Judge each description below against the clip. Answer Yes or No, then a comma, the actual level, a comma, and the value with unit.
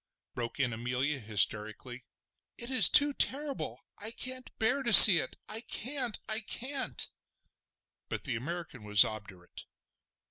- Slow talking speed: Yes, slow, 130 wpm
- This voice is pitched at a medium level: Yes, medium, 170 Hz